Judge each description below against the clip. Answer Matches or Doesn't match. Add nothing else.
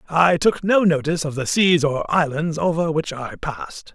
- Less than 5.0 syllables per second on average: Matches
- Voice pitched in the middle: Matches